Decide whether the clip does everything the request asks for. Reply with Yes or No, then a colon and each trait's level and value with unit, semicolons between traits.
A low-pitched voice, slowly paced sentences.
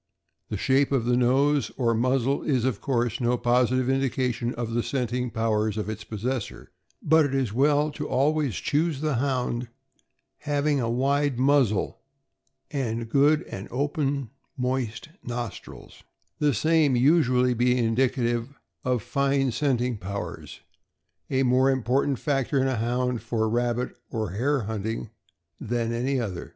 No: low, 125 Hz; average, 145 wpm